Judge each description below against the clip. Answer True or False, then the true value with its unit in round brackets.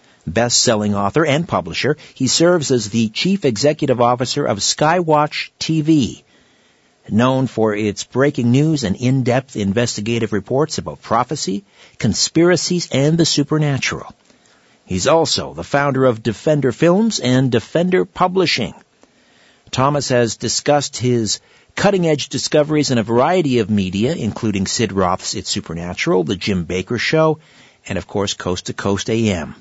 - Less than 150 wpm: True (140 wpm)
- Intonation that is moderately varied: False (5.8 semitones)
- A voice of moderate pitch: False (125 Hz)